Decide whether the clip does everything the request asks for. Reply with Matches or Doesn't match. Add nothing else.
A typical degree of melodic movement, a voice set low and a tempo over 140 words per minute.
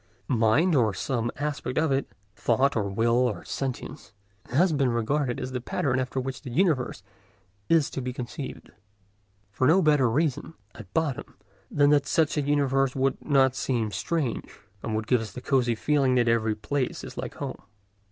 Matches